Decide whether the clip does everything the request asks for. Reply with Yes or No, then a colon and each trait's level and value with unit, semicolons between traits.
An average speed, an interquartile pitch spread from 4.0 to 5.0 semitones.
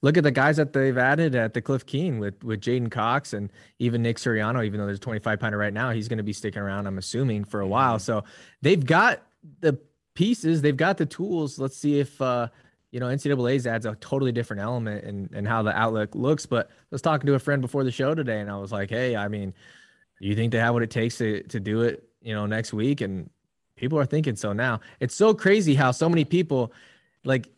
No: fast, 240 wpm; average, 4.6 semitones